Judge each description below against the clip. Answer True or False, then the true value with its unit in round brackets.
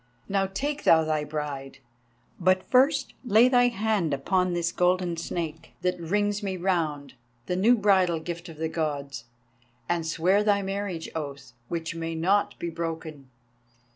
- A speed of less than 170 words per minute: True (150 wpm)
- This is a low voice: False (175 Hz)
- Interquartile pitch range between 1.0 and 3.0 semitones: False (3.7 semitones)